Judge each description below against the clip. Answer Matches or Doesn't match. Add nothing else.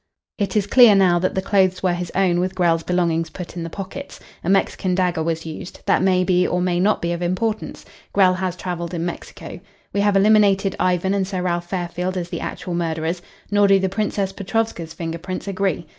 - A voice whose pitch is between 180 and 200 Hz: Matches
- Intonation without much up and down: Matches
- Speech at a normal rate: Doesn't match